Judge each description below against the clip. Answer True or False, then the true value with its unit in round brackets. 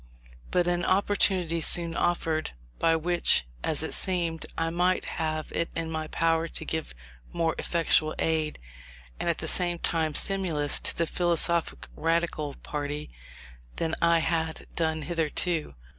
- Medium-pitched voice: True (165 Hz)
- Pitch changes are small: True (1.5 semitones)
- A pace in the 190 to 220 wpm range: False (145 wpm)